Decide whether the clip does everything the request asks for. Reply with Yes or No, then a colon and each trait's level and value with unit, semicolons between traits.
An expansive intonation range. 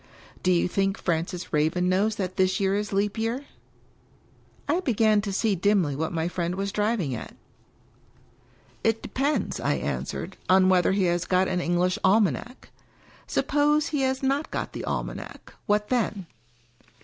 No: average, 3.7 semitones